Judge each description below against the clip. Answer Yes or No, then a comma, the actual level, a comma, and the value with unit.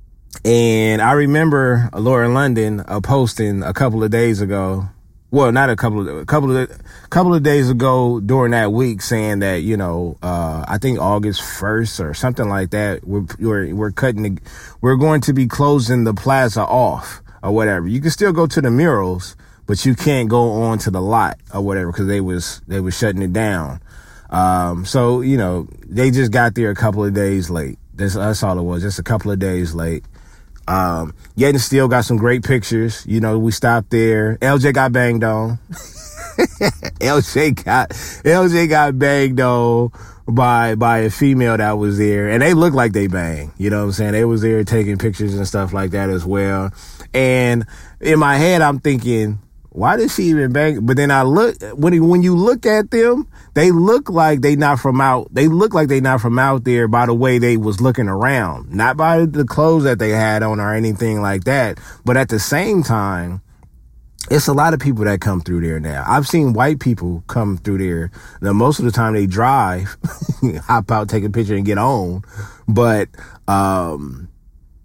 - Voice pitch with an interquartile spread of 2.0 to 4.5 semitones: No, average, 5.0 semitones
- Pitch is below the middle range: Yes, low, 110 Hz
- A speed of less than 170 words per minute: No, fast, 205 wpm